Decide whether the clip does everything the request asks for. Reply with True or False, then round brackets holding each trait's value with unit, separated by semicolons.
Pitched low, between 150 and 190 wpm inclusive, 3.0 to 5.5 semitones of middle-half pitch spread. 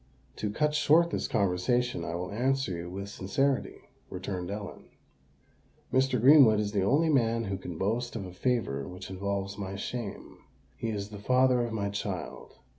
True (105 Hz; 170 wpm; 4.5 semitones)